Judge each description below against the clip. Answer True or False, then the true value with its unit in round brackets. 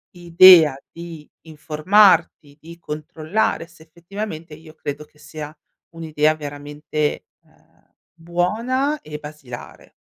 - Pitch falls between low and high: True (160 Hz)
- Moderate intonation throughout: False (2.3 semitones)